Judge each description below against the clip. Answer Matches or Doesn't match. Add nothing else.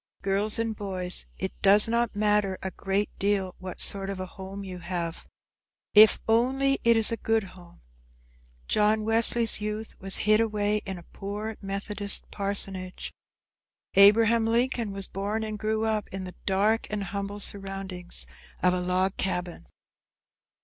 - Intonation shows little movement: Matches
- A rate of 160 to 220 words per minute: Doesn't match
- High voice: Matches